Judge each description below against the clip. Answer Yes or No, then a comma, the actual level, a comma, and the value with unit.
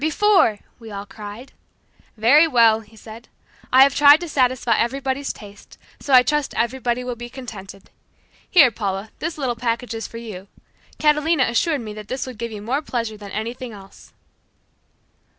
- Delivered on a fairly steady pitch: No, average, 3.8 semitones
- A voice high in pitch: Yes, high, 240 Hz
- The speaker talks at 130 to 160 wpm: No, average, 170 wpm